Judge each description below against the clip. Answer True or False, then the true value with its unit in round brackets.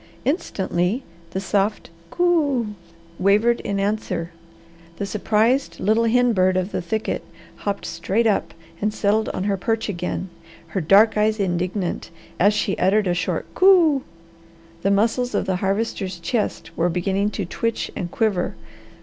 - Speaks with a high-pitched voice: True (205 Hz)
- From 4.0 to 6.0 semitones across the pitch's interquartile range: False (3.2 semitones)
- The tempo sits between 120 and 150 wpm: True (145 wpm)